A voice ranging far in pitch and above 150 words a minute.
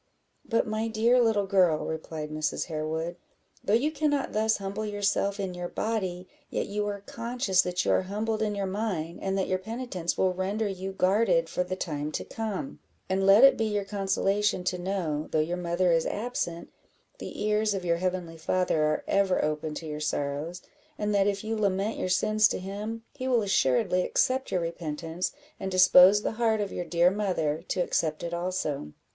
No: average, 3.7 semitones; average, 190 wpm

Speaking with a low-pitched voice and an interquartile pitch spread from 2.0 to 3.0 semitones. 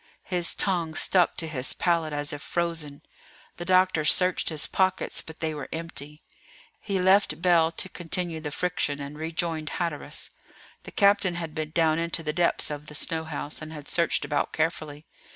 No: medium, 160 Hz; narrow, 2.5 semitones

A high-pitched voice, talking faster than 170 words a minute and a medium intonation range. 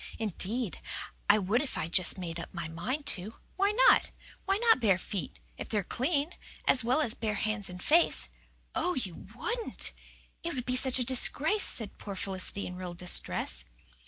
No: high, 220 Hz; average, 180 wpm; wide, 6.9 semitones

